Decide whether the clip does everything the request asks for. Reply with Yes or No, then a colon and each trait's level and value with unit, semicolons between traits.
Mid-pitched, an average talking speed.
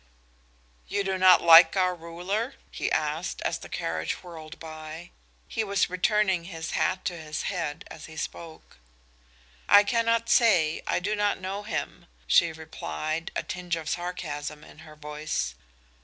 Yes: medium, 170 Hz; average, 155 wpm